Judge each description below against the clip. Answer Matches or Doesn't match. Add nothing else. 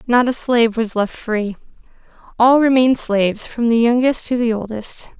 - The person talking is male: Doesn't match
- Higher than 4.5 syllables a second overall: Matches